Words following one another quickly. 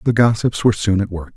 Yes: fast, 265 wpm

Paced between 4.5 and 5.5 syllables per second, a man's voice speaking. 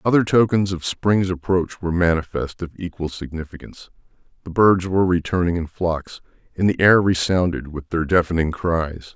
Yes: 5.1 syllables/s; male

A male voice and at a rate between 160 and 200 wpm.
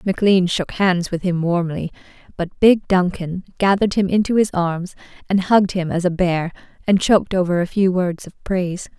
No: female; average, 185 wpm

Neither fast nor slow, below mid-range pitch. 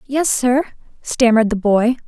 No: average, 145 wpm; high, 240 Hz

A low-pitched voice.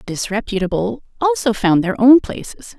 No: high, 225 Hz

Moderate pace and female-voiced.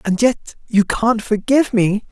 No: average, 170 wpm; male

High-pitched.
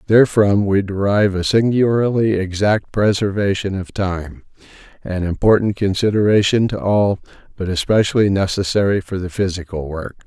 No: low, 100 Hz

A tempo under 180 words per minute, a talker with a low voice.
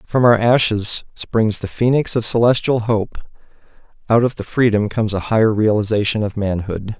Yes: average, 165 wpm; low, 110 Hz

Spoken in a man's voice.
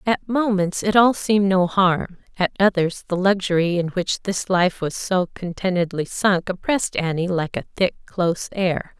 No: female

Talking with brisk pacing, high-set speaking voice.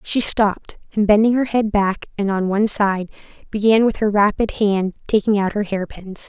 No: average, 190 wpm; high, 205 Hz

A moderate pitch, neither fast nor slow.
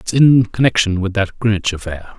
No: low, 105 Hz; average, 190 wpm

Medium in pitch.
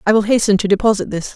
No: high, 205 Hz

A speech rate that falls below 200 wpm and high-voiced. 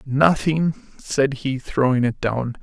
No: slow, 135 wpm; low, 135 Hz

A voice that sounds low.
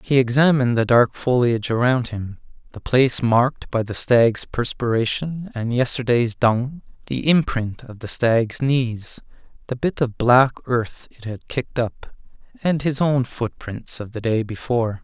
Yes: low, 120 Hz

